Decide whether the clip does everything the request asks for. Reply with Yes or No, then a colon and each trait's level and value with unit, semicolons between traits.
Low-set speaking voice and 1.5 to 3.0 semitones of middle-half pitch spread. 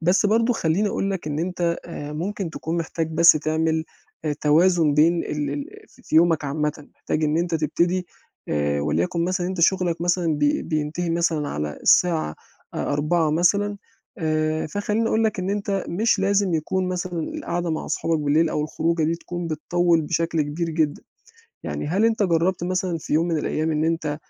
No: medium, 165 Hz; narrow, 2.6 semitones